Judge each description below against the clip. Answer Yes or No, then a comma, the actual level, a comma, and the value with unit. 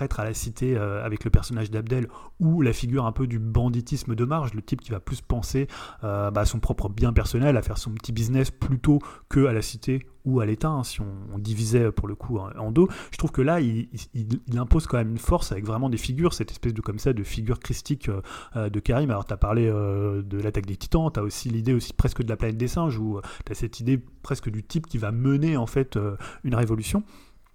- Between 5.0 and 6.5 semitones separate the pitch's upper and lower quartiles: No, average, 3.5 semitones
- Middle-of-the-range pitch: No, low, 115 Hz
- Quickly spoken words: Yes, fast, 230 wpm